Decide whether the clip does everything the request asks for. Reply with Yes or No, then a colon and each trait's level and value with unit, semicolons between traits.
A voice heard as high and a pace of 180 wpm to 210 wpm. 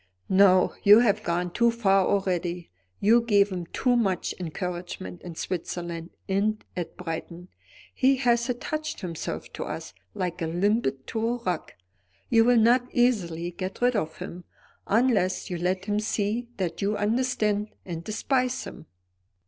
No: high, 200 Hz; average, 150 wpm